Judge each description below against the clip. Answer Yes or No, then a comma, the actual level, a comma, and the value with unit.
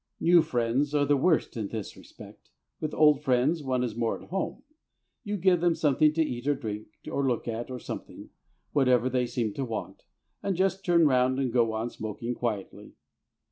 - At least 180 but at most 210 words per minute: Yes, average, 190 wpm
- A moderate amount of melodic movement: Yes, average, 4.6 semitones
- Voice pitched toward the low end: Yes, low, 130 Hz